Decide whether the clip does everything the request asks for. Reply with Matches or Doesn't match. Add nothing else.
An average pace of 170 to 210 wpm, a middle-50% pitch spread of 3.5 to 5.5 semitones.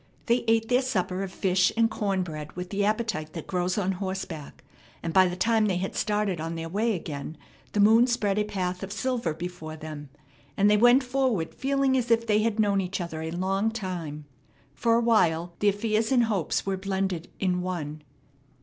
Matches